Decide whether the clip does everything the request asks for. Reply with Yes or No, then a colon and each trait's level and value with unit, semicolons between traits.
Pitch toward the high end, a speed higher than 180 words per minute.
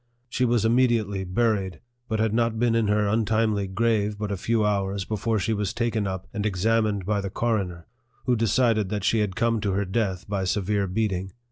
No: low, 105 Hz; average, 200 wpm